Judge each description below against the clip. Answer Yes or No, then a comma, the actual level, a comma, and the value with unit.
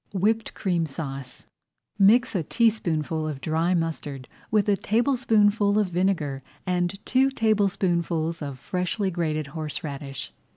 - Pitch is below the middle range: No, medium, 175 Hz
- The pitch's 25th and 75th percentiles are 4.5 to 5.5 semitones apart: Yes, average, 4.9 semitones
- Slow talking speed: Yes, slow, 120 wpm